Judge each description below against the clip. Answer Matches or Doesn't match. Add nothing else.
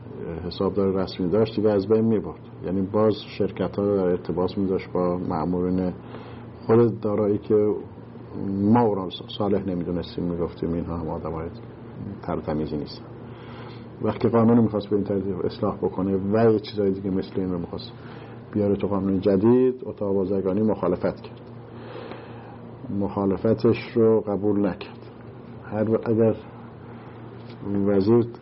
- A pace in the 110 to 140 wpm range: Matches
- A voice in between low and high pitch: Doesn't match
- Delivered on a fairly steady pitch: Doesn't match